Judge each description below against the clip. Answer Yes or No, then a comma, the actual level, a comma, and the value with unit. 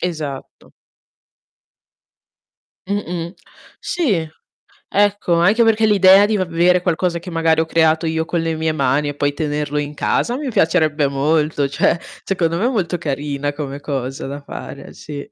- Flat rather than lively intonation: No, average, 3.7 semitones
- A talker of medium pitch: Yes, medium, 160 Hz